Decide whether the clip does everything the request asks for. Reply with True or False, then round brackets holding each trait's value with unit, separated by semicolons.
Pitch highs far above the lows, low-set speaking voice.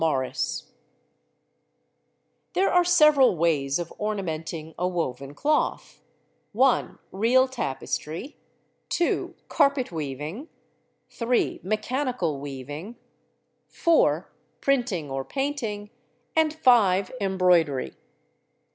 False (8.8 semitones; 195 Hz)